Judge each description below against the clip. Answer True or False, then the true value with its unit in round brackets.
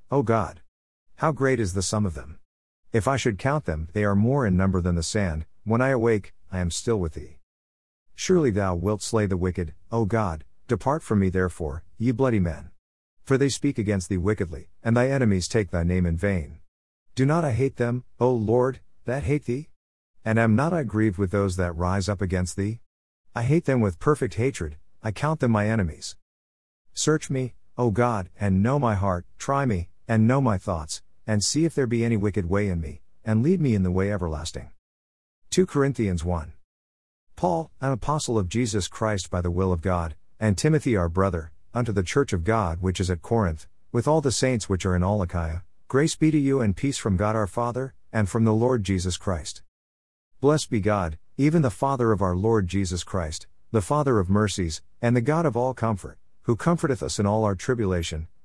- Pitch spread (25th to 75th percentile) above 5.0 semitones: True (5.6 semitones)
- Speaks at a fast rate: True (210 wpm)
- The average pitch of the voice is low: True (100 Hz)